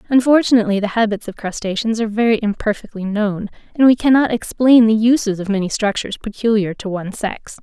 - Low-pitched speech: No, high, 215 Hz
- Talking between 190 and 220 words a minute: No, average, 175 wpm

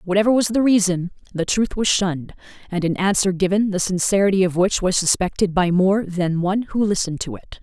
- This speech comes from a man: No, female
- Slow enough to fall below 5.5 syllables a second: No, 5.7 syllables/s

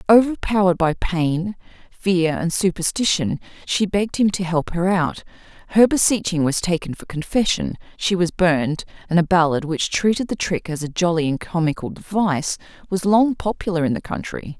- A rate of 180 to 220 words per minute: No, average, 170 wpm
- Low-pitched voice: No, medium, 180 Hz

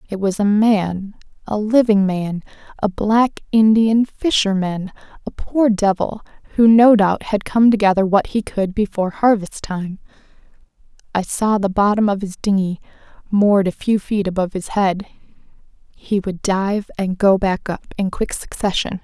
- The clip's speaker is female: Yes, female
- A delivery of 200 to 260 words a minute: No, average, 160 wpm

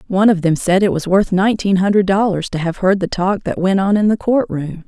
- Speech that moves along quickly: Yes, fast, 270 wpm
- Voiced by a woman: Yes, female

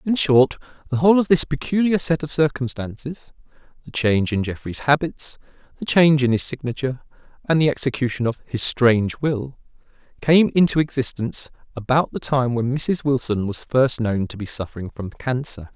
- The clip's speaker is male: Yes, male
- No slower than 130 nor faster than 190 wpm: Yes, average, 160 wpm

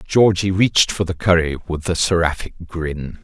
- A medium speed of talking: Yes, average, 165 wpm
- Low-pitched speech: Yes, very low, 85 Hz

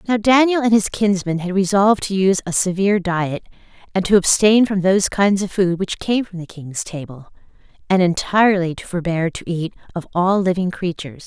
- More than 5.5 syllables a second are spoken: No, 5.4 syllables/s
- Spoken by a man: No, female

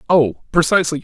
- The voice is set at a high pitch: No, medium, 160 Hz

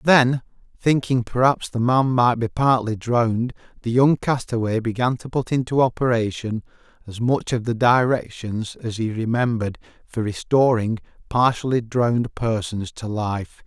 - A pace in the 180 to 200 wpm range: No, average, 140 wpm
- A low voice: Yes, low, 120 Hz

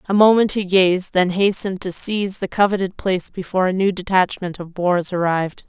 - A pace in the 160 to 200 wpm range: Yes, average, 190 wpm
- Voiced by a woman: Yes, female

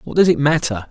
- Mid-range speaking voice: Yes, medium, 150 Hz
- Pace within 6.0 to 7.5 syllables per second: Yes, 6.2 syllables/s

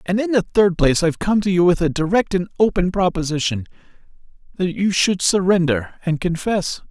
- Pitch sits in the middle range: Yes, medium, 180 Hz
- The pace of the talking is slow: No, average, 175 wpm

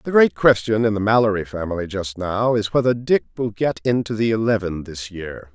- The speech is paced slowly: No, fast, 205 wpm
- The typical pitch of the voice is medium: No, low, 105 Hz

